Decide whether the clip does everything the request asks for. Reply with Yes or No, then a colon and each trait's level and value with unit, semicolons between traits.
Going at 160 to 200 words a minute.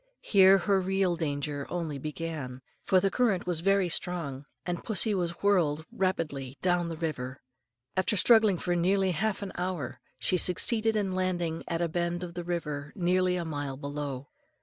Yes: average, 170 wpm